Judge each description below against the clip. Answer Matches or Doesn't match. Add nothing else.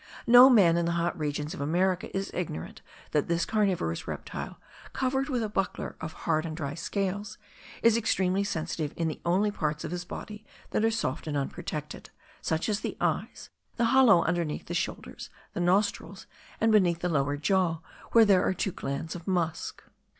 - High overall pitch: Doesn't match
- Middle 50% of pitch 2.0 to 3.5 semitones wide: Doesn't match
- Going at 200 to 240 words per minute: Doesn't match